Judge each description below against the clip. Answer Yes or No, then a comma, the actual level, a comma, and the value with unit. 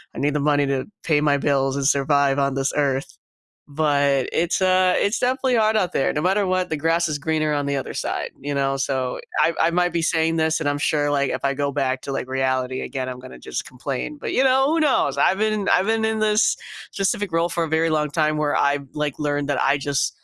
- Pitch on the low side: No, medium, 150 Hz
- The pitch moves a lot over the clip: No, average, 4.2 semitones